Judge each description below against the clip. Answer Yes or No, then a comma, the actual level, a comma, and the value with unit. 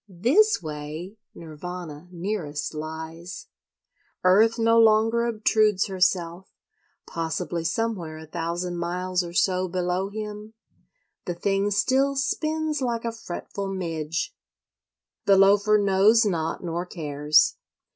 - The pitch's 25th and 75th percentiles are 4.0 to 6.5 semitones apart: Yes, average, 4.4 semitones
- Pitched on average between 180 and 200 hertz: Yes, medium, 185 Hz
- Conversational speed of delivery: No, slow, 110 wpm